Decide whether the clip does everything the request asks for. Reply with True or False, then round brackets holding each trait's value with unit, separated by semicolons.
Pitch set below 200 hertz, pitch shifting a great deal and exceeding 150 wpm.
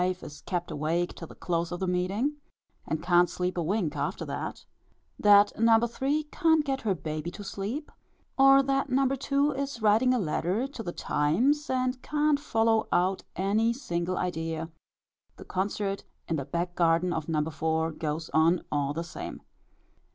True (185 Hz; 7.4 semitones; 170 wpm)